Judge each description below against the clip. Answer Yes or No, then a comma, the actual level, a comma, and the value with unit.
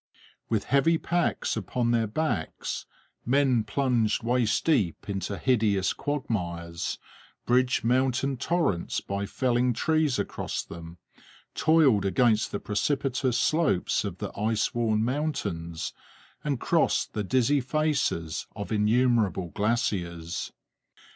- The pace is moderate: No, slow, 110 wpm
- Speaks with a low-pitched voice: Yes, low, 120 Hz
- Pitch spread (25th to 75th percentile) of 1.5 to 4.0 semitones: No, average, 5.2 semitones